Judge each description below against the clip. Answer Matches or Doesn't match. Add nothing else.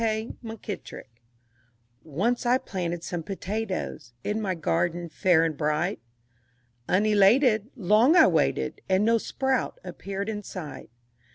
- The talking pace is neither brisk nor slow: Doesn't match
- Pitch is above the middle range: Matches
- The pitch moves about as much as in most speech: Matches